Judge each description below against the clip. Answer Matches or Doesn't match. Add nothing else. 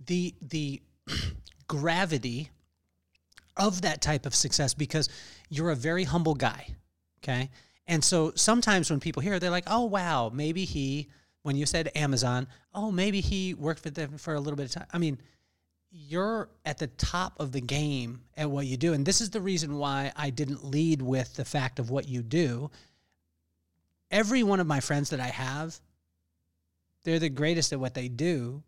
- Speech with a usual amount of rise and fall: Matches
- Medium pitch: Matches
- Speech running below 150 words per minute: Doesn't match